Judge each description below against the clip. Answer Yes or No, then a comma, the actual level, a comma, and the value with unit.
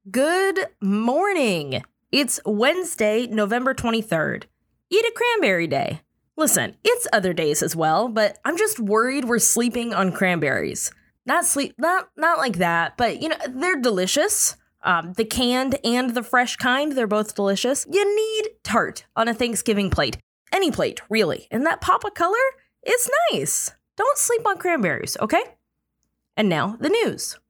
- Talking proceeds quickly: No, average, 155 wpm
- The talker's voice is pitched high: Yes, very high, 250 Hz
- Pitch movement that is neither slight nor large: No, wide, 8.4 semitones